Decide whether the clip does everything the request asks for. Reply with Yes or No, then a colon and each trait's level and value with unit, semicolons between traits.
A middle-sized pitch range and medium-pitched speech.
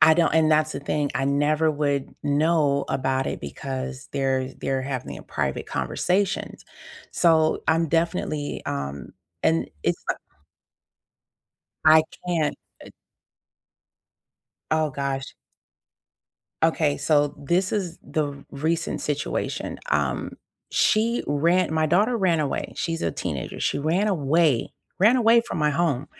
Yes: average, 3.1 semitones; medium, 155 Hz